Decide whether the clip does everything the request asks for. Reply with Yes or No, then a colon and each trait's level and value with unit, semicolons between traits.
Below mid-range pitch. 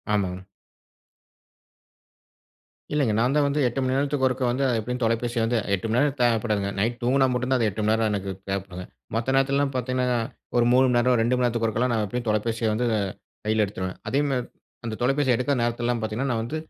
Yes: low, 120 Hz